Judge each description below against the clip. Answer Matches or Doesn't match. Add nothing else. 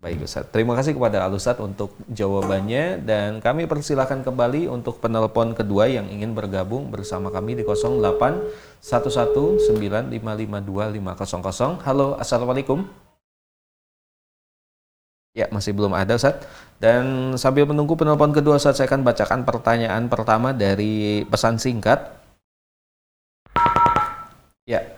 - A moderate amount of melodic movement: Matches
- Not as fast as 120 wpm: Matches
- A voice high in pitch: Doesn't match